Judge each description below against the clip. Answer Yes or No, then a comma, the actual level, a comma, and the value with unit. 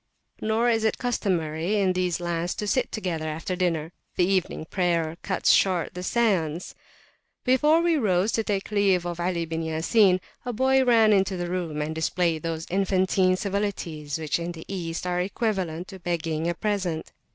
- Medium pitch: Yes, medium, 180 Hz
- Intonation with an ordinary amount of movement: Yes, average, 3.6 semitones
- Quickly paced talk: No, average, 175 wpm